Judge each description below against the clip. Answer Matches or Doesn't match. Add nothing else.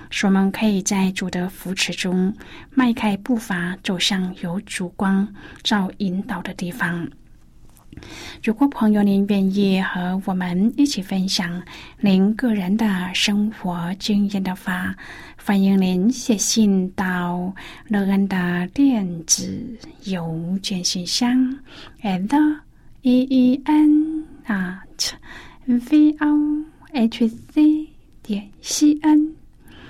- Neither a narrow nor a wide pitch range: Matches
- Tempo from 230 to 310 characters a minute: Doesn't match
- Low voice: Doesn't match